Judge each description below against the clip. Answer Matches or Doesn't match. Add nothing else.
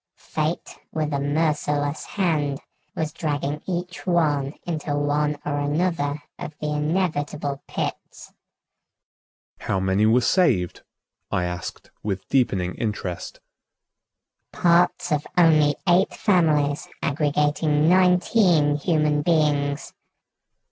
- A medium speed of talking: Doesn't match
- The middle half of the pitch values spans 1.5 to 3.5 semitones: Matches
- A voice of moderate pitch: Matches